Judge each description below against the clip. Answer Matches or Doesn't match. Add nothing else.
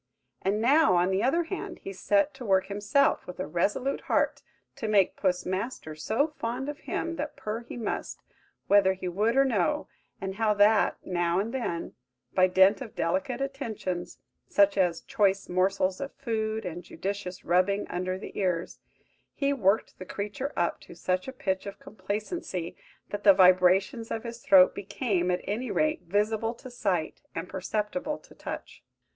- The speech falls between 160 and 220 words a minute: Matches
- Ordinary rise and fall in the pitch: Matches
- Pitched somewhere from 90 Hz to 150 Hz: Doesn't match